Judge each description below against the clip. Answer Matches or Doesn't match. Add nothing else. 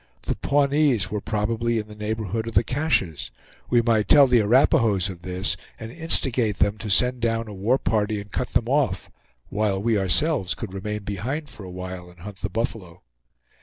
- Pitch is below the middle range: Matches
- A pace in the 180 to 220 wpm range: Matches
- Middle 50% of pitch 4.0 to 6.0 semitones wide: Doesn't match